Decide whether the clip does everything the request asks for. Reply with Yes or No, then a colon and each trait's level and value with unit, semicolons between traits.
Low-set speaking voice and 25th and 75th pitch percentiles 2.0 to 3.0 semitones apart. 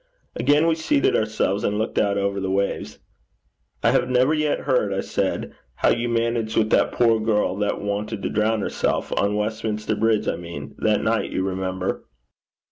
Yes: low, 105 Hz; average, 2.7 semitones